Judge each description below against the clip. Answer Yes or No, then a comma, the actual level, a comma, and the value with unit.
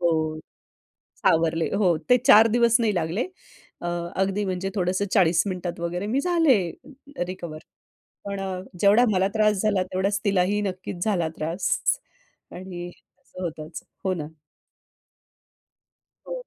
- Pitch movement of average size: Yes, average, 3.0 semitones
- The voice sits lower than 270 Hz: Yes, medium, 185 Hz